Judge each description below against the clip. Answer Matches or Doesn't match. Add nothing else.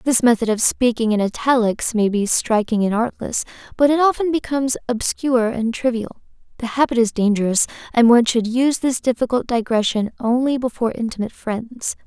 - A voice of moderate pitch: Doesn't match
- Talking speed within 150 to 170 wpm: Matches